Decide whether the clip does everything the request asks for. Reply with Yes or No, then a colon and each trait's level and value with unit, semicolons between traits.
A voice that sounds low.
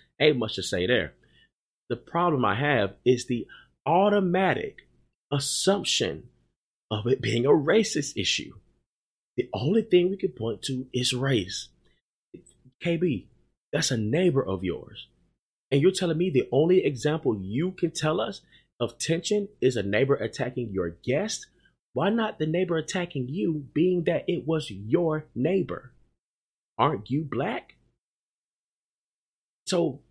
No: medium, 150 Hz